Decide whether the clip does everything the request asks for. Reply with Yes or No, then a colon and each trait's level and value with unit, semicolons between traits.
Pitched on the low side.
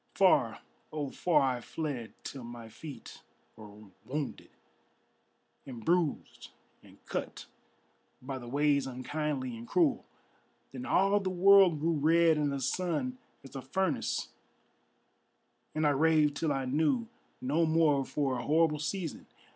No: medium, 150 Hz